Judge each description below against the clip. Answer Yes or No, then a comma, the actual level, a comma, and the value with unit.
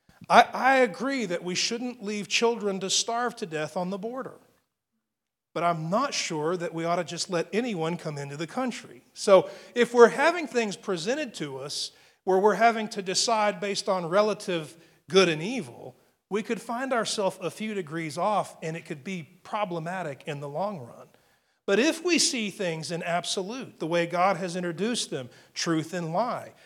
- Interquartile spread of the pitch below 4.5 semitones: No, average, 5.0 semitones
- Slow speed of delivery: No, average, 180 wpm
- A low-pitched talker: No, high, 190 Hz